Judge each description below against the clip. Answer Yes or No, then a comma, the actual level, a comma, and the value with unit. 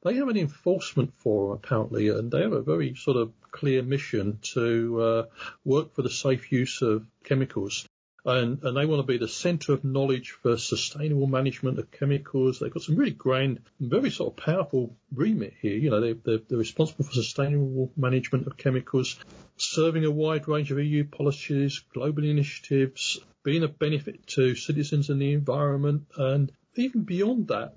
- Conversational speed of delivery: Yes, average, 180 wpm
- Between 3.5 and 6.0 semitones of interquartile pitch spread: No, average, 2.8 semitones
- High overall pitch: No, medium, 140 Hz